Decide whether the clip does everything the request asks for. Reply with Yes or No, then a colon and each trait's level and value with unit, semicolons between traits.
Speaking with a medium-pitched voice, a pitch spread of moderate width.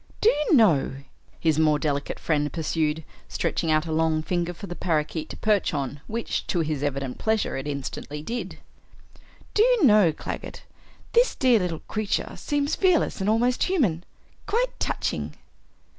No: medium, 170 Hz; wide, 7.2 semitones